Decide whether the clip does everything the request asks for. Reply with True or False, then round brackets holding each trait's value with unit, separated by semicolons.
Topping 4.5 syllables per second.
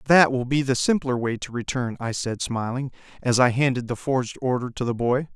True (5.5 syllables/s)